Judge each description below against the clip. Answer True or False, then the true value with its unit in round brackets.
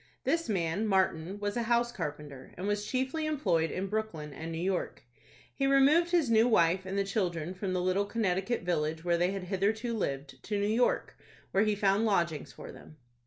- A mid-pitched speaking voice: False (195 Hz)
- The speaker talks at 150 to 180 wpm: False (195 wpm)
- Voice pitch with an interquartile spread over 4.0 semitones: True (4.6 semitones)